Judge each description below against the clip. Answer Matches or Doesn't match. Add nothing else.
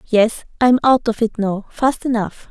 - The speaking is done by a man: Doesn't match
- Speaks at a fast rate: Doesn't match